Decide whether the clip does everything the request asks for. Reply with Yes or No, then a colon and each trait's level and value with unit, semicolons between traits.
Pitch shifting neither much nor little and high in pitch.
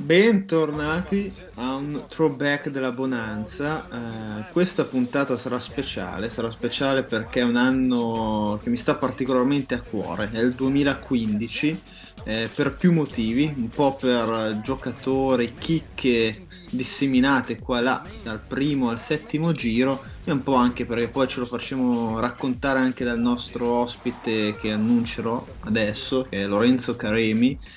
No: average, 3.1 semitones; low, 125 Hz